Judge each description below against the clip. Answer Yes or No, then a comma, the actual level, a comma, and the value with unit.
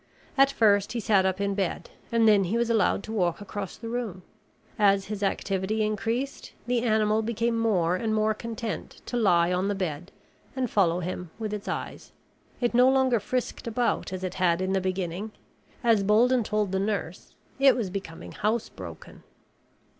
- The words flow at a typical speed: Yes, average, 175 wpm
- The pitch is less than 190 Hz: No, high, 210 Hz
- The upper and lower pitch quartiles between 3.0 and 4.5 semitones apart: Yes, average, 3.4 semitones